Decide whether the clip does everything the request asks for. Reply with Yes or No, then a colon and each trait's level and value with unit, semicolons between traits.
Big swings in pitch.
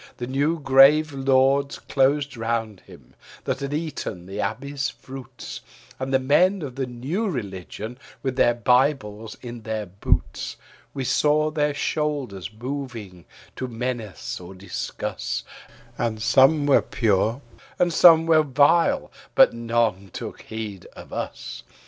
No: average, 4.4 semitones